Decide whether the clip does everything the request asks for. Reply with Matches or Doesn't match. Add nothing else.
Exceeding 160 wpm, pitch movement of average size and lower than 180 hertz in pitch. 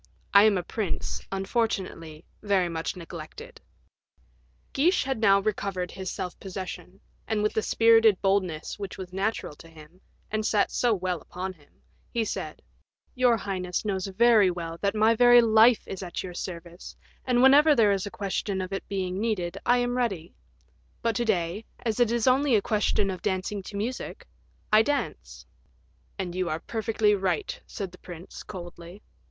Doesn't match